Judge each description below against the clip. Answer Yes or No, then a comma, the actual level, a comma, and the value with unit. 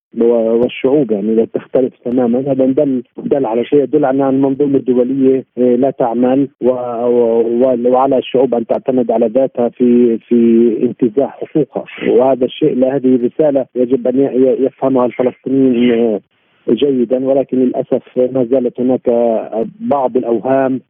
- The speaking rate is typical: Yes, average, 120 wpm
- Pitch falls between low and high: No, low, 125 Hz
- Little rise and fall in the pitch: Yes, narrow, 1.7 semitones